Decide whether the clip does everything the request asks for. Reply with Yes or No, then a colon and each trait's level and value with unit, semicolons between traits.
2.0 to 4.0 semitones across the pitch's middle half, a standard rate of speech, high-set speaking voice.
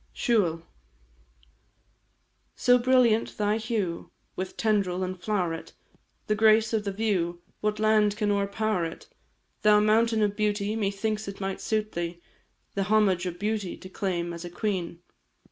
Yes: average, 2.8 semitones; average, 145 wpm; high, 205 Hz